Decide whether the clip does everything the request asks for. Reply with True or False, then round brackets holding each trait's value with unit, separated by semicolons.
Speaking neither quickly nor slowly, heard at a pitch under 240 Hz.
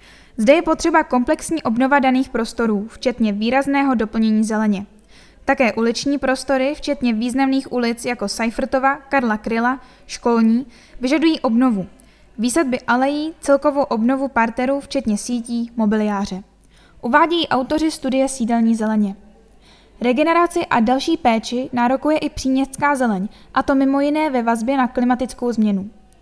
False (125 wpm; 250 Hz)